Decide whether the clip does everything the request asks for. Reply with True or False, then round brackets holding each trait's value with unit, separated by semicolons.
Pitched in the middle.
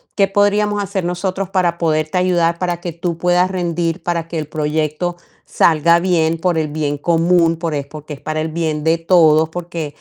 True (170 Hz)